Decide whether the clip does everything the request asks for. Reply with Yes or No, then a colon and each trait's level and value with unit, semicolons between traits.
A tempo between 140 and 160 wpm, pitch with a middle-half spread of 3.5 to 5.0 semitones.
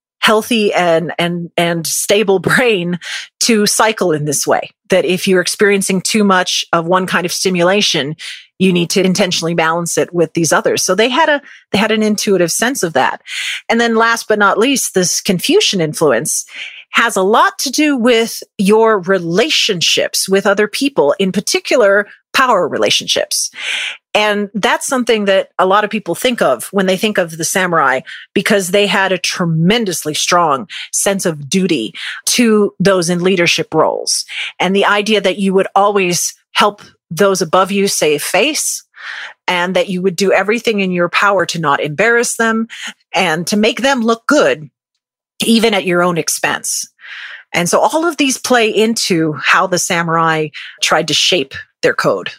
No: average, 170 wpm; average, 4.1 semitones